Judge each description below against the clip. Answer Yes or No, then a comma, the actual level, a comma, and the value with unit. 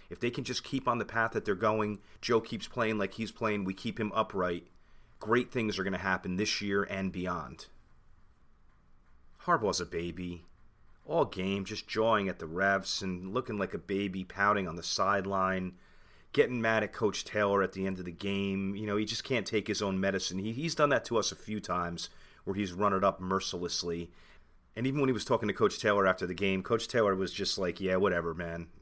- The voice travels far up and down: No, average, 2.9 semitones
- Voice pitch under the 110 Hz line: Yes, low, 100 Hz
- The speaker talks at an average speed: No, fast, 220 wpm